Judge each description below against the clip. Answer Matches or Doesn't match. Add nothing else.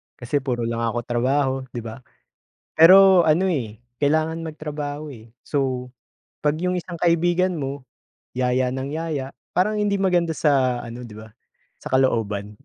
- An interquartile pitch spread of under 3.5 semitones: Doesn't match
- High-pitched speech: Doesn't match